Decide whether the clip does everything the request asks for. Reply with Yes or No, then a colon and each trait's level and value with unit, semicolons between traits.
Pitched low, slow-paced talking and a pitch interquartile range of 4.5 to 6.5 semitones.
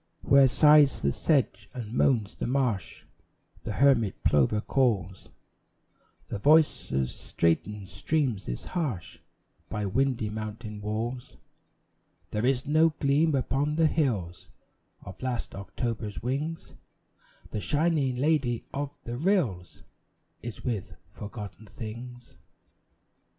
Yes: low, 120 Hz; slow, 115 wpm; average, 5.0 semitones